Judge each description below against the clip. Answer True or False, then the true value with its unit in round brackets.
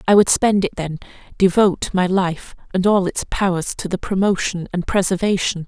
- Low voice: False (185 Hz)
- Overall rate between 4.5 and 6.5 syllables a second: True (5.1 syllables/s)